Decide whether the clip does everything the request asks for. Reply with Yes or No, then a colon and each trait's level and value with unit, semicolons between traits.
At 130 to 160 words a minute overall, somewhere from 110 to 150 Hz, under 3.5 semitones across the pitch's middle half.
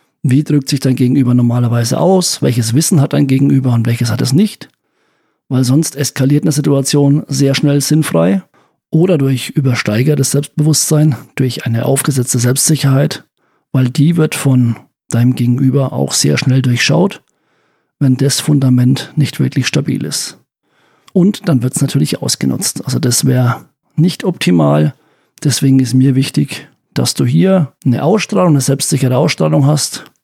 Yes: average, 145 wpm; low, 135 Hz; average, 2.9 semitones